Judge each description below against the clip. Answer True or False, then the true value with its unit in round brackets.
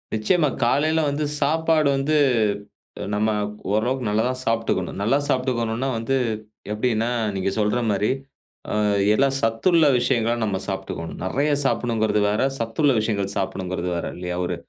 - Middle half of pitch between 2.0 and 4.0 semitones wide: False (4.6 semitones)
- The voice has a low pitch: True (115 Hz)